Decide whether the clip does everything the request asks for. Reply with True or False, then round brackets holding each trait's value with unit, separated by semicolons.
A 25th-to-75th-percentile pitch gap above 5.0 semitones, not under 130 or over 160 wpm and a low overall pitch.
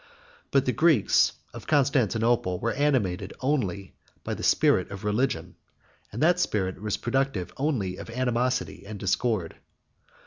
True (5.4 semitones; 135 wpm; 115 Hz)